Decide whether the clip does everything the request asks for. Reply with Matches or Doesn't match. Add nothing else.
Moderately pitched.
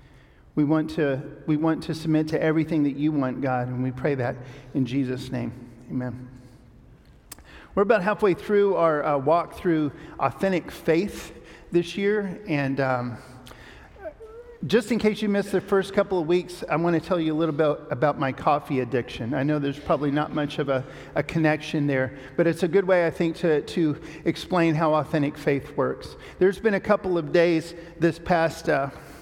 Matches